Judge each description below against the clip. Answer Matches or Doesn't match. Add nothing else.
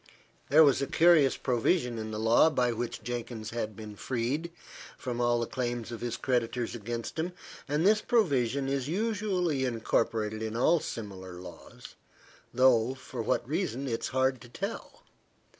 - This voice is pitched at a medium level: Doesn't match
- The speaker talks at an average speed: Matches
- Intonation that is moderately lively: Matches